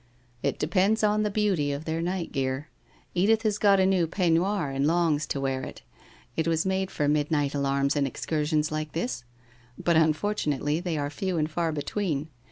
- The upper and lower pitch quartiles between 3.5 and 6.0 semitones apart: Yes, average, 4.5 semitones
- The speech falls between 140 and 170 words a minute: No, average, 190 wpm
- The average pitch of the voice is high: No, medium, 160 Hz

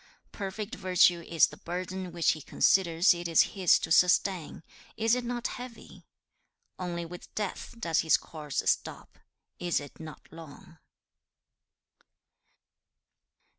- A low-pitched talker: No, medium, 175 Hz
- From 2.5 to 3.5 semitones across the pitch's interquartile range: Yes, average, 2.8 semitones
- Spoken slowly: Yes, slow, 125 wpm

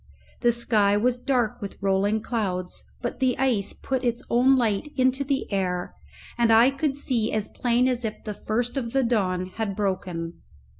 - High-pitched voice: Yes, high, 230 Hz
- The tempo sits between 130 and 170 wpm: No, average, 180 wpm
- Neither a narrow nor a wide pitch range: Yes, average, 4.0 semitones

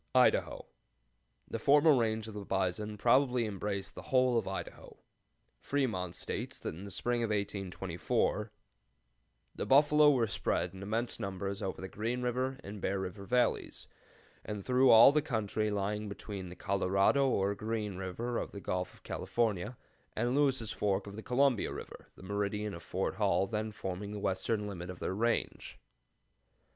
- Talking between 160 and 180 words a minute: Yes, average, 165 wpm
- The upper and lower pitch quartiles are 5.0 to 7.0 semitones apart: No, average, 3.7 semitones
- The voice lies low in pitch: Yes, low, 105 Hz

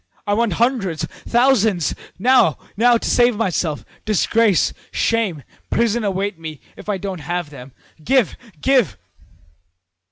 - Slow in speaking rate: Yes, slow, 125 wpm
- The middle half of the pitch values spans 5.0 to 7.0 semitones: Yes, wide, 5.5 semitones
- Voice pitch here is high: Yes, high, 205 Hz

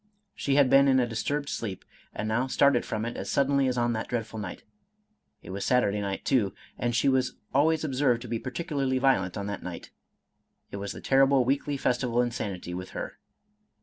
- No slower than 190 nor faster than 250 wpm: Yes, fast, 205 wpm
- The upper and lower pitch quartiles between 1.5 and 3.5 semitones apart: No, average, 3.9 semitones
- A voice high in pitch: No, low, 125 Hz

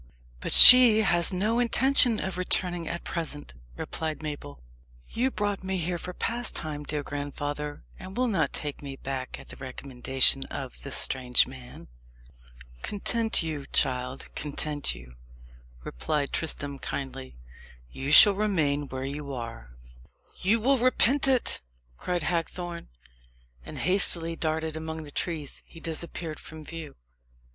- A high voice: No, medium, 160 Hz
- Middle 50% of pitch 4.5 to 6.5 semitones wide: Yes, average, 5.0 semitones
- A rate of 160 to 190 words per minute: No, slow, 135 wpm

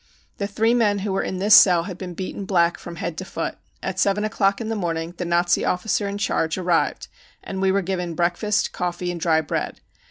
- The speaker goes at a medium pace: No, fast, 220 wpm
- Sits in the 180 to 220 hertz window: Yes, medium, 185 Hz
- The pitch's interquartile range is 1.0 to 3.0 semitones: Yes, narrow, 2.6 semitones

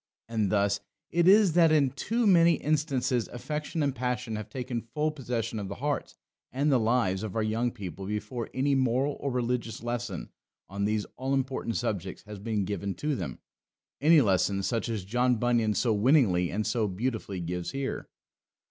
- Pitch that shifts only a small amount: No, average, 4.6 semitones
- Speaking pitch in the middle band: No, low, 120 Hz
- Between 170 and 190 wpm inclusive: Yes, average, 175 wpm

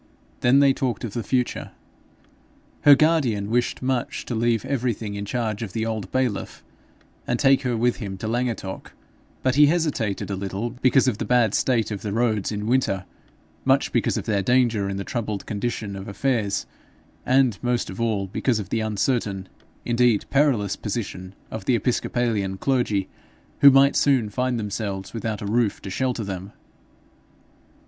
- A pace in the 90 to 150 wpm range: No, average, 170 wpm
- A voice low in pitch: Yes, low, 115 Hz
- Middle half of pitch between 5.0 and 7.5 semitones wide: No, average, 3.8 semitones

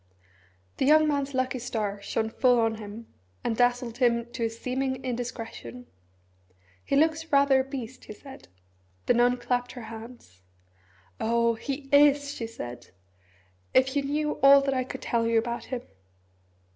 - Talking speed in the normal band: Yes, average, 160 wpm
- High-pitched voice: Yes, high, 245 Hz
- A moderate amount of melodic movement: Yes, average, 3.1 semitones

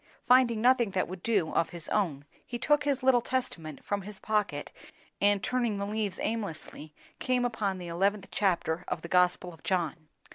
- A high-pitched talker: Yes, high, 200 Hz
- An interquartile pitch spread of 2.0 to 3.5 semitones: No, average, 5.0 semitones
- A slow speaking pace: No, average, 180 wpm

